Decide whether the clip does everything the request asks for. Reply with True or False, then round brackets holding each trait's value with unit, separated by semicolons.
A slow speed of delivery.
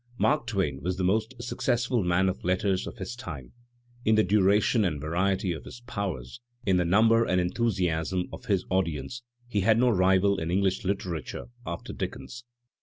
False (175 wpm)